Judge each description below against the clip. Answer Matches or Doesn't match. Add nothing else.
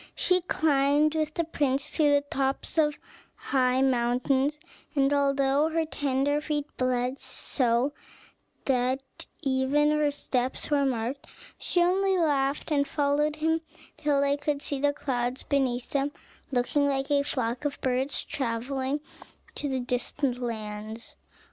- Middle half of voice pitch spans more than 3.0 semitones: Doesn't match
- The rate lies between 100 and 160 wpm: Matches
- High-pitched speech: Matches